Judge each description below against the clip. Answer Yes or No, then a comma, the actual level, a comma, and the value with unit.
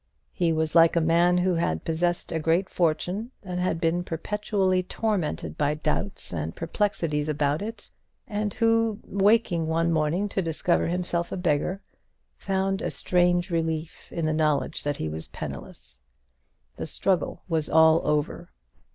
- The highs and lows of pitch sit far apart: No, average, 3.3 semitones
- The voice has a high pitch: No, medium, 170 Hz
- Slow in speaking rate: No, average, 150 wpm